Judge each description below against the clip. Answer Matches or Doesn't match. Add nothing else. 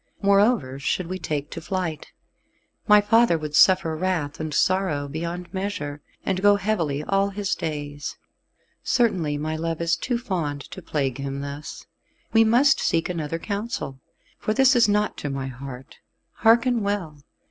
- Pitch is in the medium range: Matches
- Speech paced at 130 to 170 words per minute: Matches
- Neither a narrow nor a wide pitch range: Doesn't match